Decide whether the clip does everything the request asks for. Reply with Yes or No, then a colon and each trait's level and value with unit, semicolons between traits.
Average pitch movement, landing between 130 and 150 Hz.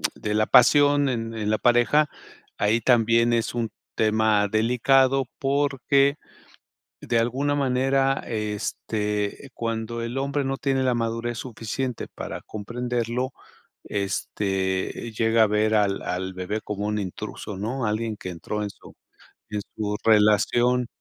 No: average, 3.2 semitones; low, 115 Hz